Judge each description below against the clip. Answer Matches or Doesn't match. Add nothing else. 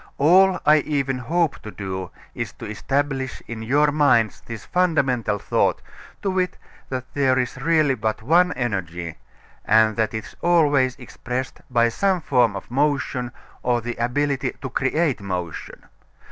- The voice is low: Matches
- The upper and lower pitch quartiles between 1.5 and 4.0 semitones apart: Doesn't match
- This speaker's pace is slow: Doesn't match